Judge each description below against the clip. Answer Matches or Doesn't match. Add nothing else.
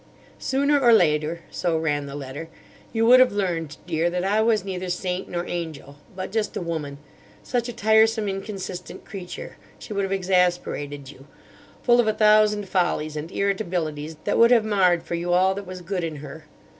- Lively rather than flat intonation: Doesn't match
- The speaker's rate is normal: Matches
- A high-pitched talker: Doesn't match